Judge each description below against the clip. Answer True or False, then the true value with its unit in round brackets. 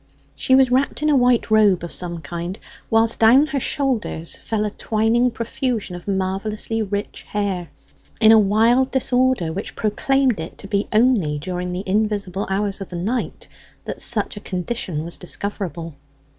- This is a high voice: True (210 Hz)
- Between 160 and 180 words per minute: True (165 wpm)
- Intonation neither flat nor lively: True (4.5 semitones)